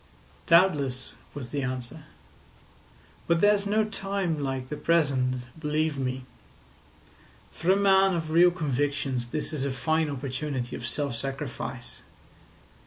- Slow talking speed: Yes, slow, 125 wpm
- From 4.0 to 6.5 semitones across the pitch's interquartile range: Yes, average, 4.5 semitones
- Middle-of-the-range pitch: Yes, medium, 145 Hz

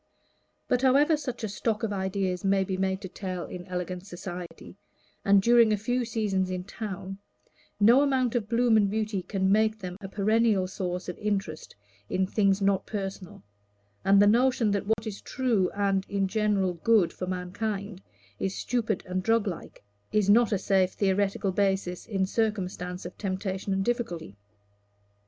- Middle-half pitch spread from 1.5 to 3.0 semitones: Yes, average, 2.7 semitones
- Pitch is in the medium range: No, high, 200 Hz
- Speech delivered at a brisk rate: No, average, 165 wpm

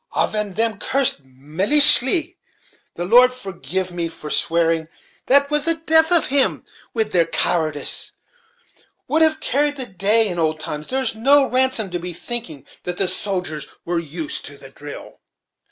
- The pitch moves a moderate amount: No, wide, 8.2 semitones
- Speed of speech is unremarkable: Yes, average, 155 wpm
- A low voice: No, high, 200 Hz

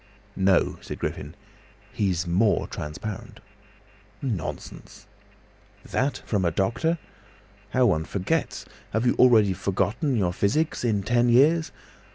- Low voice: Yes, low, 105 Hz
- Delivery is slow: Yes, slow, 115 wpm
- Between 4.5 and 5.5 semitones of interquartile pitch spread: Yes, average, 5.1 semitones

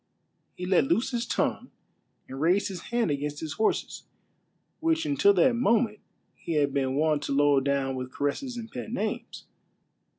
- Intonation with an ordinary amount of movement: No, wide, 8.7 semitones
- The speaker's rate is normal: Yes, average, 165 wpm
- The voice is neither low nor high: Yes, medium, 170 Hz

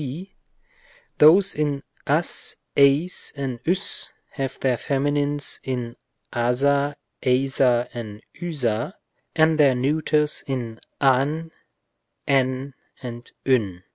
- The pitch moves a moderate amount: Yes, average, 3.1 semitones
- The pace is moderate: No, slow, 100 wpm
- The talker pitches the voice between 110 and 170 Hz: Yes, low, 135 Hz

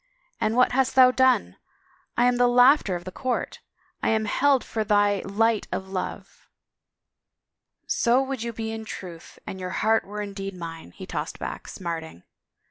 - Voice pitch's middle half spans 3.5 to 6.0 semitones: Yes, average, 4.4 semitones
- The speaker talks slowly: No, average, 190 wpm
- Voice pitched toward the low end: No, high, 220 Hz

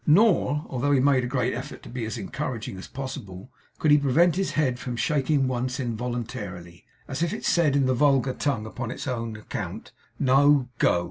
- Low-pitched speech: Yes, low, 130 Hz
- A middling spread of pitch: Yes, average, 3.2 semitones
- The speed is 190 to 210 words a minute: Yes, average, 195 wpm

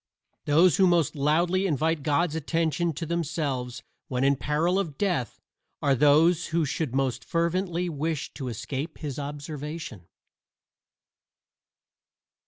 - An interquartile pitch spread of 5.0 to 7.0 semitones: No, average, 3.3 semitones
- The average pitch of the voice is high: No, medium, 155 Hz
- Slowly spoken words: Yes, slow, 120 wpm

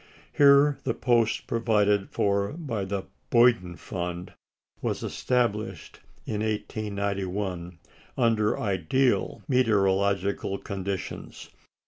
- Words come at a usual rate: No, slow, 85 wpm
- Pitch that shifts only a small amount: No, average, 3.2 semitones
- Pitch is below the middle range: Yes, low, 105 Hz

